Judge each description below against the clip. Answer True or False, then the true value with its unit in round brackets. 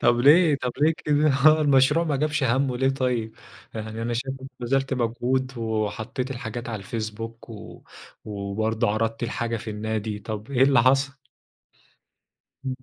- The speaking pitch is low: True (120 Hz)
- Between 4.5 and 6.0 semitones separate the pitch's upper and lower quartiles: False (3.4 semitones)